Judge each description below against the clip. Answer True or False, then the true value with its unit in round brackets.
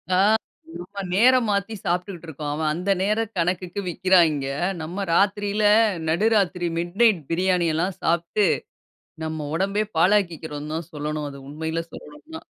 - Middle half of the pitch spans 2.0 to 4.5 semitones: True (4.0 semitones)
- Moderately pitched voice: True (180 Hz)